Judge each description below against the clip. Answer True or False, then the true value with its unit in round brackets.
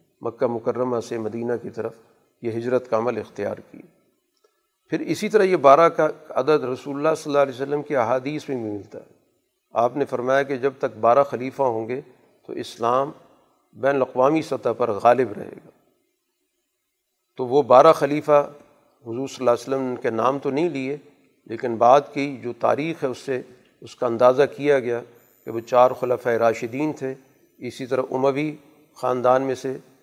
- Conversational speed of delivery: True (180 wpm)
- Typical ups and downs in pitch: True (3.0 semitones)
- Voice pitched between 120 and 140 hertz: True (135 Hz)